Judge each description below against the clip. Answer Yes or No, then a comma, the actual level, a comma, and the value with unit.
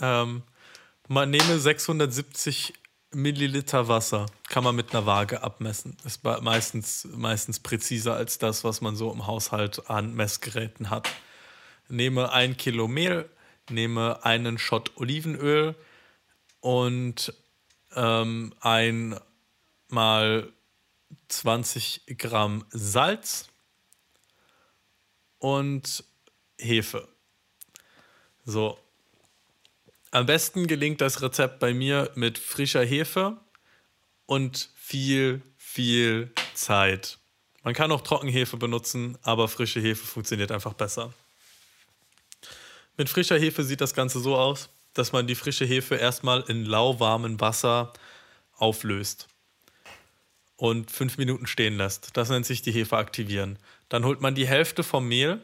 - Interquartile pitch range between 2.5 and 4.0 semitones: Yes, average, 3.3 semitones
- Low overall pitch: Yes, low, 120 Hz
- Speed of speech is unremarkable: No, slow, 115 wpm